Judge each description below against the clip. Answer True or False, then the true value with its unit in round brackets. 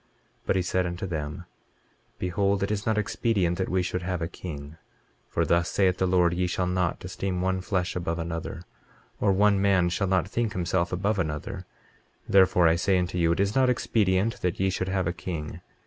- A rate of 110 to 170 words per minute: False (205 wpm)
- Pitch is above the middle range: False (90 Hz)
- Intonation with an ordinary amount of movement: False (2.0 semitones)